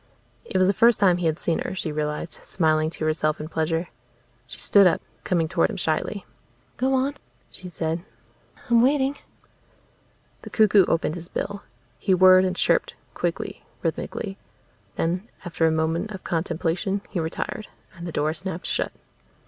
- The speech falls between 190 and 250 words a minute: No, average, 165 wpm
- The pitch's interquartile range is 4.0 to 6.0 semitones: No, average, 3.6 semitones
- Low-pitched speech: No, medium, 175 Hz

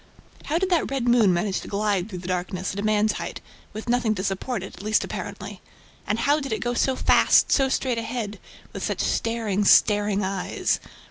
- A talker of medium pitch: No, high, 215 Hz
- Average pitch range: Yes, average, 3.7 semitones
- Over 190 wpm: Yes, fast, 205 wpm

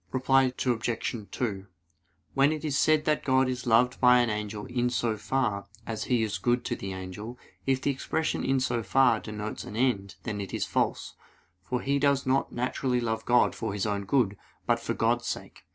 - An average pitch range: Yes, average, 3.7 semitones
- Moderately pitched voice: No, low, 120 Hz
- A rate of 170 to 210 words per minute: Yes, average, 200 wpm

